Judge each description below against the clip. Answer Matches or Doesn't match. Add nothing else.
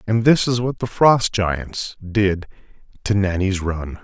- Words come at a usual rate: Matches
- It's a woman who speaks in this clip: Doesn't match